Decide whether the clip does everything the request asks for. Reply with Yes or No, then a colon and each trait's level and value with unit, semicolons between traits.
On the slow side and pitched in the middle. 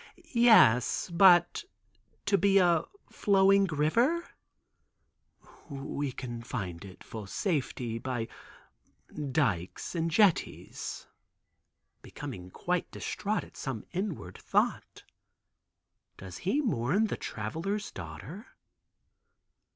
Yes: slow, 90 wpm; medium, 160 Hz